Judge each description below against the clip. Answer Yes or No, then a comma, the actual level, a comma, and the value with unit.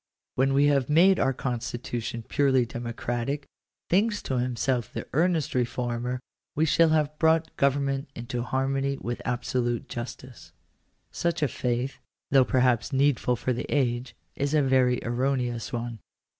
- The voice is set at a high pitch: No, low, 130 Hz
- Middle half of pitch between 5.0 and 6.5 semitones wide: No, average, 2.8 semitones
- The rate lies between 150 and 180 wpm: No, average, 140 wpm